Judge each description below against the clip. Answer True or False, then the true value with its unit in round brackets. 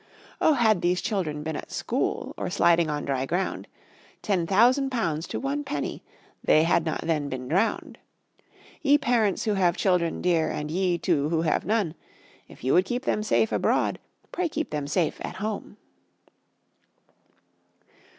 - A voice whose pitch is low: False (180 Hz)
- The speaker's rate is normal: True (160 wpm)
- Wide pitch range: True (5.7 semitones)